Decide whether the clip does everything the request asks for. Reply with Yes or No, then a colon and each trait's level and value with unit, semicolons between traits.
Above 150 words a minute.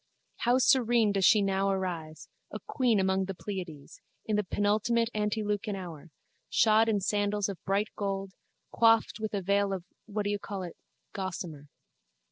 Yes: average, 160 wpm